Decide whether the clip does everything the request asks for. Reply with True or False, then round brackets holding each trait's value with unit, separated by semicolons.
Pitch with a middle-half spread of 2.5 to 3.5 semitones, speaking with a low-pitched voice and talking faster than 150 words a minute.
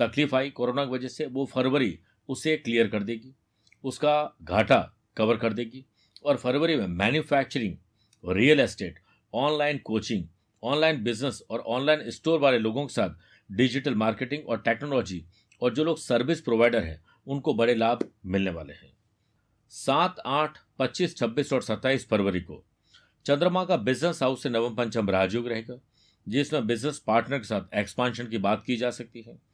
False (4.3 semitones; 120 Hz; 160 wpm)